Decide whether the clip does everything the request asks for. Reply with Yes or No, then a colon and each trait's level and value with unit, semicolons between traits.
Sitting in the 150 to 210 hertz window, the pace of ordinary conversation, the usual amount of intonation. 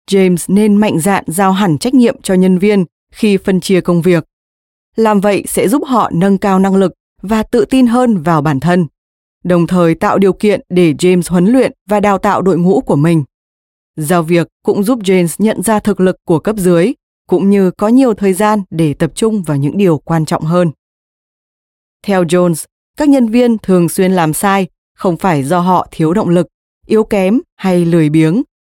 Yes: medium, 185 Hz; average, 200 wpm; average, 3.7 semitones